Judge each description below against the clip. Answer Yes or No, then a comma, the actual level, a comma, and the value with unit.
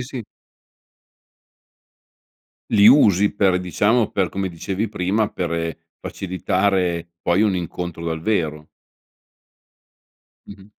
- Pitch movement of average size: Yes, average, 3.1 semitones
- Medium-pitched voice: No, very low, 95 Hz